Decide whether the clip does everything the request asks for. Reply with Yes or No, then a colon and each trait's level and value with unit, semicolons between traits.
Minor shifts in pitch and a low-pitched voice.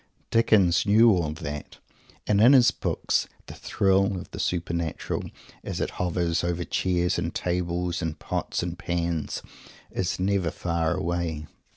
Yes: narrow, 2.2 semitones; very low, 90 Hz